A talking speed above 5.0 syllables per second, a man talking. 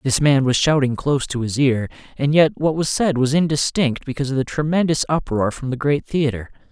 Yes: 5.6 syllables/s; male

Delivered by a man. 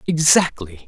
Yes: male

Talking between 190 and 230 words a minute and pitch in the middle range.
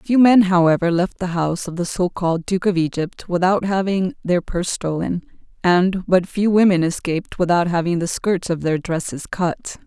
No: average, 180 wpm; medium, 180 Hz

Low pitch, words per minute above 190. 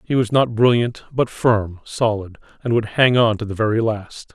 Yes: low, 115 Hz; fast, 205 wpm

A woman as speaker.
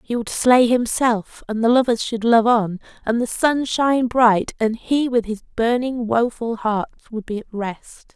Yes: female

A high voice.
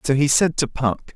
No: medium, 140 Hz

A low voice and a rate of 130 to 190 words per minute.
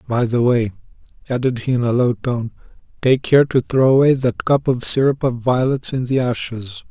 No: low, 125 Hz; average, 200 wpm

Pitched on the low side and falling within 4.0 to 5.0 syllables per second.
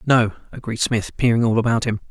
No: low, 115 Hz; 6.0 syllables/s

